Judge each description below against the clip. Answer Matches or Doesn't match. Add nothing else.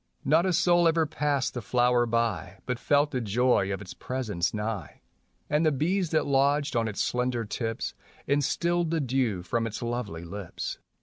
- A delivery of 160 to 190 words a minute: Matches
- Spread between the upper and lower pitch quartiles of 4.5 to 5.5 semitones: Matches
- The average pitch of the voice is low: Matches